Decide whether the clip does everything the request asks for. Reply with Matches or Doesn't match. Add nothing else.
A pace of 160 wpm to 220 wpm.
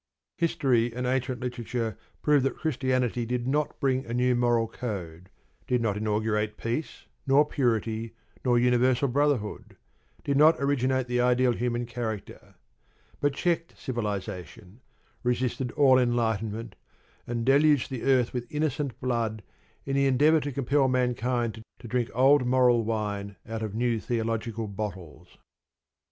Doesn't match